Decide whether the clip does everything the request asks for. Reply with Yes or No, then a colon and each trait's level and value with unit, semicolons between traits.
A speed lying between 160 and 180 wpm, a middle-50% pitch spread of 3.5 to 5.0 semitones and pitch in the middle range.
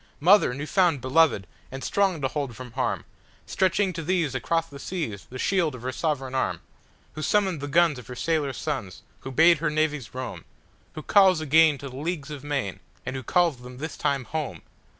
No: average, 190 wpm; average, 4.2 semitones; medium, 150 Hz